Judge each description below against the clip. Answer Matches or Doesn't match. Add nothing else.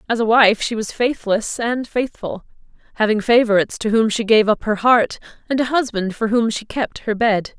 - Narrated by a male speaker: Doesn't match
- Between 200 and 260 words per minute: Matches